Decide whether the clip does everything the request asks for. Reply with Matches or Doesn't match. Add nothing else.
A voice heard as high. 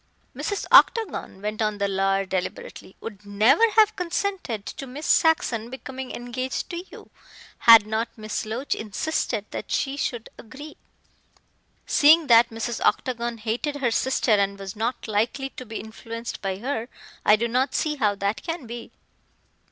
Matches